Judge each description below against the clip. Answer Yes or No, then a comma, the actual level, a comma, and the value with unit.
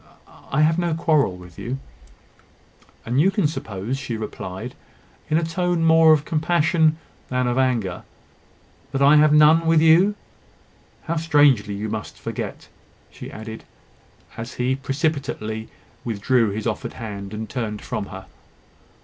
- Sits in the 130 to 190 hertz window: Yes, low, 135 Hz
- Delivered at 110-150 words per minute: Yes, average, 140 wpm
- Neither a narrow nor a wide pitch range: No, wide, 6.3 semitones